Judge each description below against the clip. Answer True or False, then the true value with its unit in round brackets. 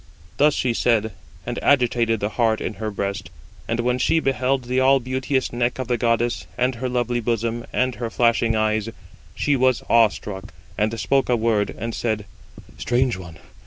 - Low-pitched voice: True (120 Hz)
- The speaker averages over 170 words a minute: True (180 wpm)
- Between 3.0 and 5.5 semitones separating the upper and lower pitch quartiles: False (2.5 semitones)